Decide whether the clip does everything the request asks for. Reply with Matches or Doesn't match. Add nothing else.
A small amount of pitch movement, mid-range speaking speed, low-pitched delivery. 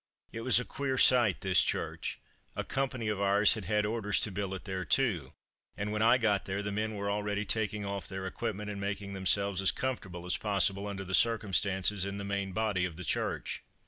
Doesn't match